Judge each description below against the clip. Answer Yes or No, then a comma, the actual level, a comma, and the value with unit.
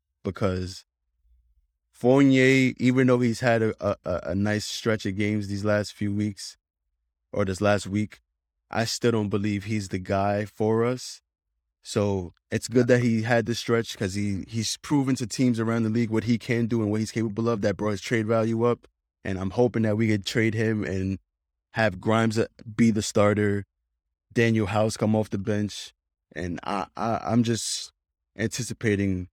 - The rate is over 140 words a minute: Yes, average, 180 wpm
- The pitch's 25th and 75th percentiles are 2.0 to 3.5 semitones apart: Yes, average, 3.2 semitones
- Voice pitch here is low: Yes, low, 105 Hz